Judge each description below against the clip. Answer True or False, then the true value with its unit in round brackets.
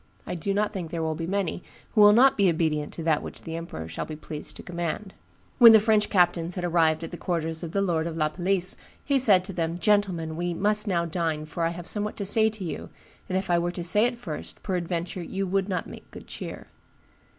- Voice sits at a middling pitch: True (175 Hz)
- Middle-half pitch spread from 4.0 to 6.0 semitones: False (3.3 semitones)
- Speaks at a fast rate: True (240 wpm)